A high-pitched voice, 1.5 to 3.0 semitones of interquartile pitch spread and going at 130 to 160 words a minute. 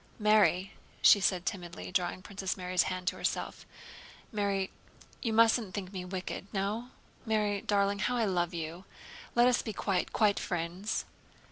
Yes: high, 195 Hz; narrow, 2.6 semitones; average, 150 wpm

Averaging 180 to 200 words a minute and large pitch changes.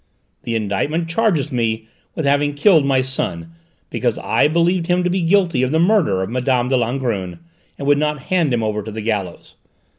Yes: average, 190 wpm; wide, 6.7 semitones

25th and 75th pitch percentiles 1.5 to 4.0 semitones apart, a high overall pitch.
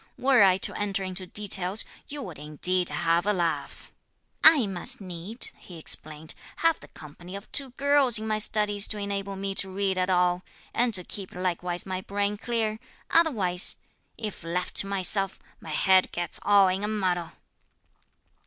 Yes: average, 2.7 semitones; high, 195 Hz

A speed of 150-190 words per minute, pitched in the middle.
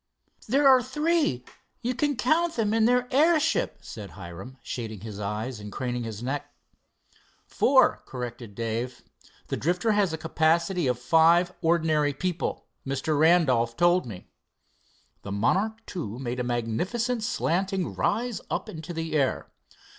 No: average, 140 wpm; medium, 160 Hz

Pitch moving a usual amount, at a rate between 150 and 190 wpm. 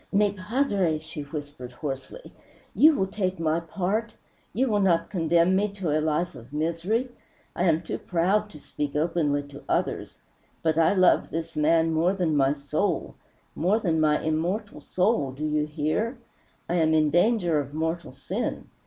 Yes: average, 4.0 semitones; average, 170 wpm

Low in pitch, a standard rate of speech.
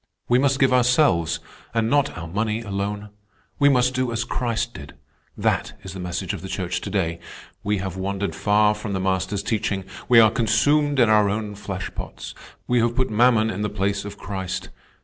Yes: low, 105 Hz; average, 190 wpm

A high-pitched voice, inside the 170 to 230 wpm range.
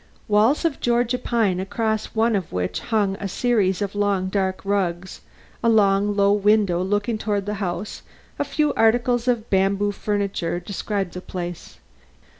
No: high, 205 Hz; average, 155 wpm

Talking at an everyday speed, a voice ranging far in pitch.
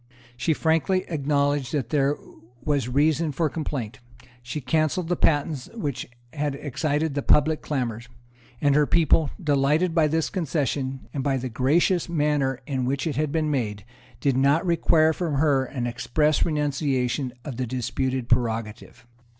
No: average, 150 wpm; average, 3.2 semitones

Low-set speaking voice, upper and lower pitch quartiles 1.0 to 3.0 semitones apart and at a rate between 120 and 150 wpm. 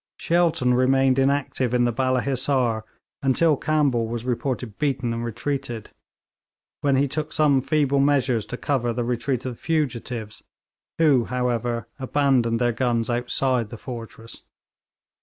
Yes: low, 130 Hz; average, 2.7 semitones; average, 140 wpm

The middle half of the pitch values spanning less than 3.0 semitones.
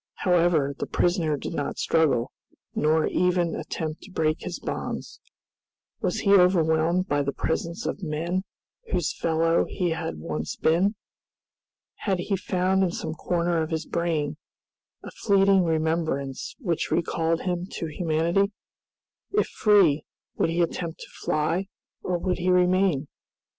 Yes: narrow, 2.4 semitones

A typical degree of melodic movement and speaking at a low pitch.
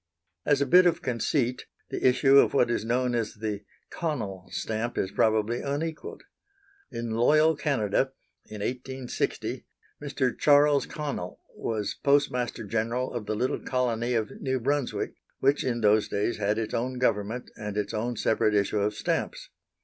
Yes: average, 3.9 semitones; low, 120 Hz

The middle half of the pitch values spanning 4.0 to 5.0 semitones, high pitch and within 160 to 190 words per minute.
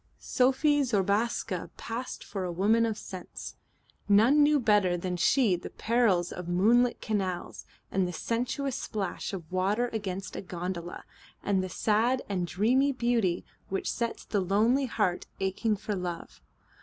No: average, 4.5 semitones; high, 205 Hz; average, 145 wpm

